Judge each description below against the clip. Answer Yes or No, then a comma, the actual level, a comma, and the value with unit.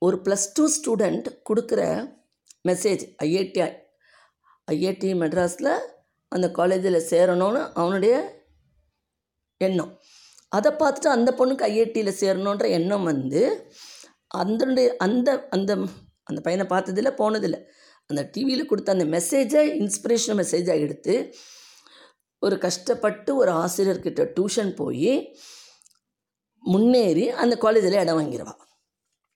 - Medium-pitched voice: No, high, 195 Hz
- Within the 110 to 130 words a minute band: No, average, 100 wpm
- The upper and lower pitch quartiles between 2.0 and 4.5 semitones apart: No, wide, 5.5 semitones